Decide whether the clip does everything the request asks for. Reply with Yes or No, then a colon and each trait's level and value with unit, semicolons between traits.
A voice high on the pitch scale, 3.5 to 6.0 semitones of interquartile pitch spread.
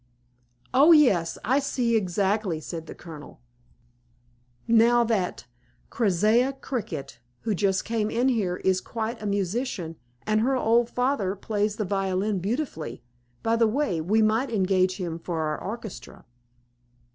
Yes: high, 210 Hz; average, 4.2 semitones